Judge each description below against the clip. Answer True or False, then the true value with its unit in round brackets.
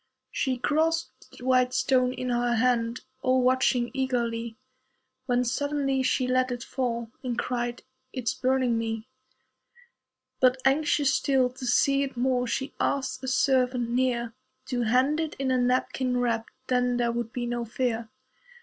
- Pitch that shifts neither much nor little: False (1.5 semitones)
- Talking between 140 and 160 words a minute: True (150 wpm)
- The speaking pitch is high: True (250 Hz)